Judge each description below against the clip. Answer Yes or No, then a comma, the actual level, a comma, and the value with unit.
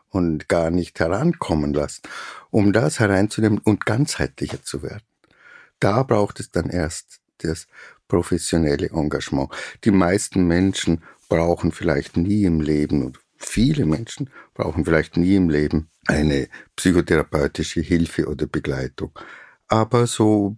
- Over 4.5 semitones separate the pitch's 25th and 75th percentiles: Yes, average, 5.0 semitones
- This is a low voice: Yes, very low, 85 Hz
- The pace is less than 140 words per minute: Yes, slow, 125 wpm